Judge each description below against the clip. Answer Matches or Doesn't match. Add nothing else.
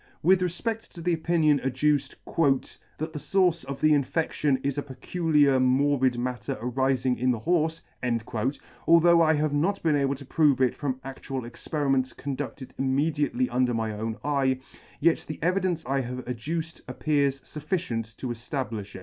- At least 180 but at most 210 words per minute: Doesn't match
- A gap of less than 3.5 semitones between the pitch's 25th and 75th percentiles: Doesn't match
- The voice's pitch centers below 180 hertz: Matches